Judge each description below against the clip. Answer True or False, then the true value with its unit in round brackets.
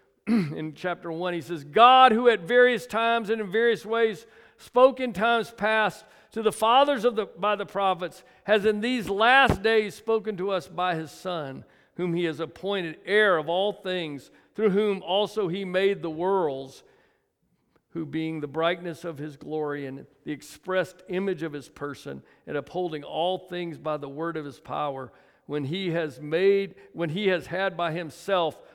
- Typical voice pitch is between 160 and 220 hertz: True (185 Hz)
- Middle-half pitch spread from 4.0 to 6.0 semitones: True (4.9 semitones)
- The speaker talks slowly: False (180 wpm)